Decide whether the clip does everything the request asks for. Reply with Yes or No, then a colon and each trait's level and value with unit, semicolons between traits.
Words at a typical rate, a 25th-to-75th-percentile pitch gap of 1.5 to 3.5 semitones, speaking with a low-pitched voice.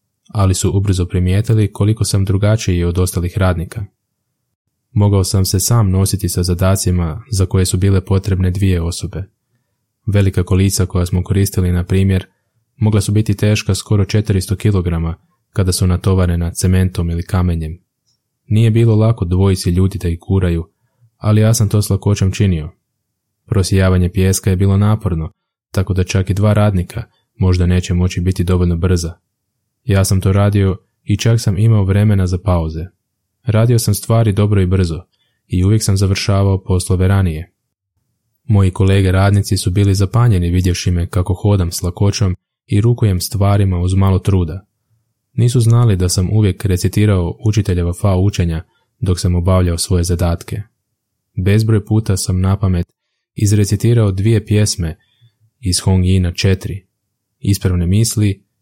Yes: average, 145 wpm; average, 2.7 semitones; low, 100 Hz